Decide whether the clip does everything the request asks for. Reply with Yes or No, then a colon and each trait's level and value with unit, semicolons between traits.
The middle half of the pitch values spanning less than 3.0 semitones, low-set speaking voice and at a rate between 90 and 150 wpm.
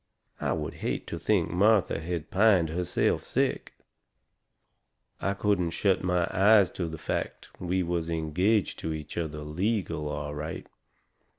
No: average, 3.4 semitones; very low, 85 Hz; average, 140 wpm